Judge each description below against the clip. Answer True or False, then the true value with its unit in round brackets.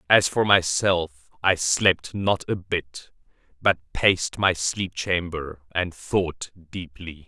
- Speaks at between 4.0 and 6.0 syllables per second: False (3.2 syllables/s)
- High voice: False (85 Hz)